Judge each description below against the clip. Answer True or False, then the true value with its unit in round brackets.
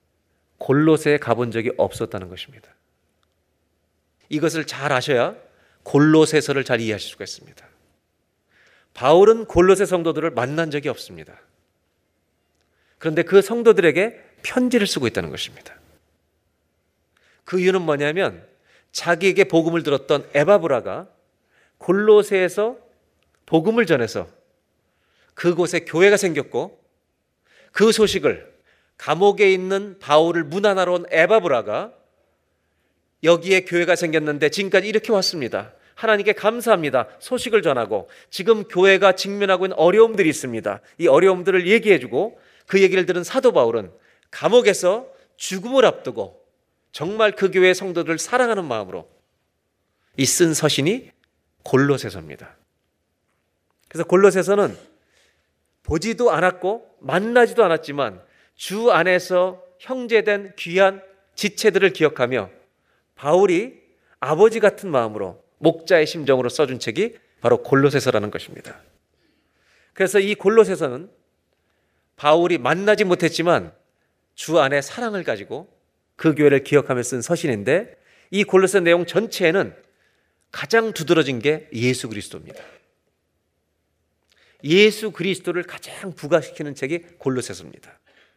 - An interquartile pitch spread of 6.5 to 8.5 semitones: True (8.0 semitones)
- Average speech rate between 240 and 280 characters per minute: False (290 characters per minute)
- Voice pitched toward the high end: False (170 Hz)